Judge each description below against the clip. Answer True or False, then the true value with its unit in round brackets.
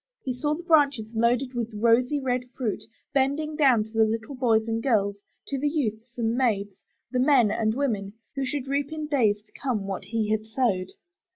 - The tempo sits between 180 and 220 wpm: True (195 wpm)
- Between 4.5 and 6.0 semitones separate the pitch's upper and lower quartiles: False (3.9 semitones)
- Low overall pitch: False (240 Hz)